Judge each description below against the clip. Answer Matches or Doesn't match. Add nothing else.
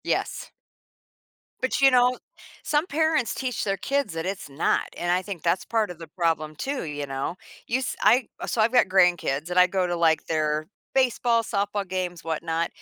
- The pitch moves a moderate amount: Doesn't match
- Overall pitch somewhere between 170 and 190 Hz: Matches